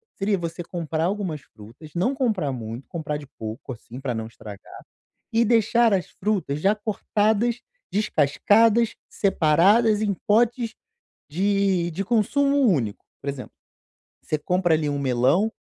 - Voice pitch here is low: No, medium, 185 Hz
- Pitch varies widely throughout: Yes, wide, 6.9 semitones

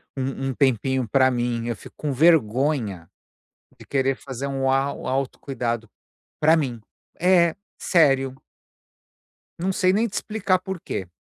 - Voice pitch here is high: No, low, 135 Hz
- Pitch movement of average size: Yes, average, 4.4 semitones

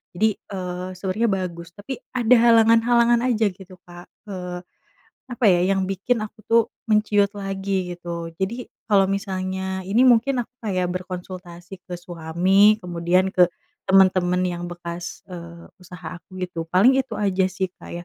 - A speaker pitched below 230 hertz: Yes, high, 190 Hz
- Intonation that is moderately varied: Yes, average, 3.1 semitones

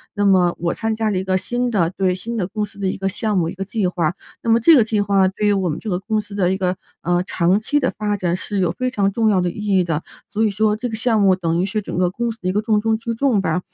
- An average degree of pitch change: Yes, average, 3.1 semitones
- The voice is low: No, high, 200 Hz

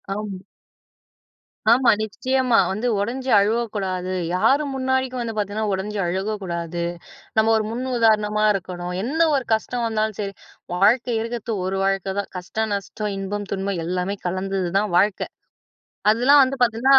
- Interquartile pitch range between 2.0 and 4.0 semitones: Yes, average, 3.7 semitones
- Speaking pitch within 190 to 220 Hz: Yes, high, 210 Hz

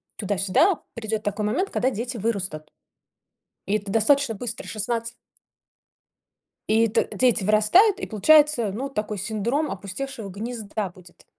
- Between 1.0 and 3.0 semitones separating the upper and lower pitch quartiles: No, average, 3.5 semitones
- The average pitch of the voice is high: Yes, high, 220 Hz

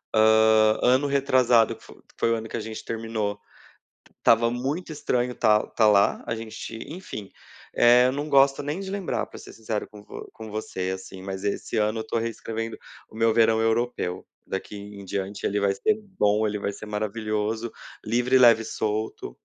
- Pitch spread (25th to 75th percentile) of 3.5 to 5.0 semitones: No, narrow, 2.5 semitones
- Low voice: Yes, low, 110 Hz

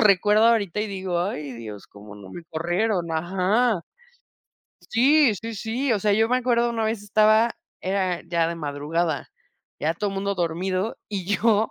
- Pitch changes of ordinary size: Yes, average, 4.6 semitones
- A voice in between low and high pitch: No, high, 195 Hz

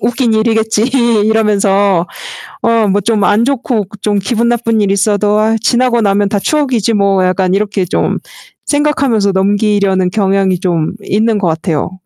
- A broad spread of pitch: No, narrow, 2.6 semitones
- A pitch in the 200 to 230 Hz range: Yes, high, 205 Hz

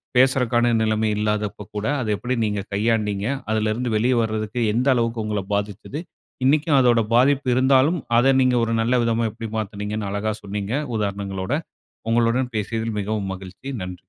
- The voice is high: No, low, 110 Hz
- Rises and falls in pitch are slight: No, average, 3.0 semitones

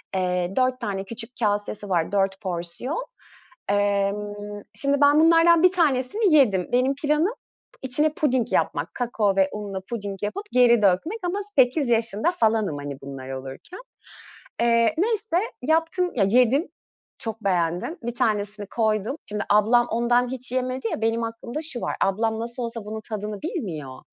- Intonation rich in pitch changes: No, average, 5.0 semitones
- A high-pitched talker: Yes, high, 230 Hz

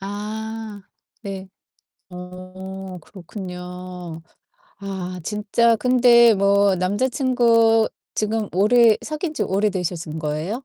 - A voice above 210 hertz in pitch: No, high, 200 Hz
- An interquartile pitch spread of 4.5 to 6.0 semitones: No, average, 3.6 semitones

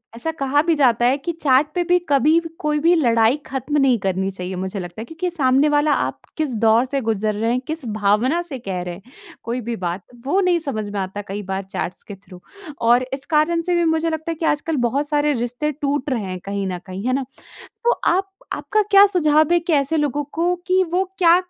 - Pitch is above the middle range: Yes, very high, 275 Hz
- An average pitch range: No, wide, 6.5 semitones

